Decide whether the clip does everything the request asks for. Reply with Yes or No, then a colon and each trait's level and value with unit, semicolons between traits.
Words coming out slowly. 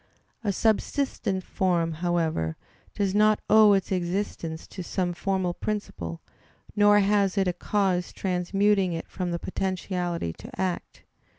Yes: slow, 125 wpm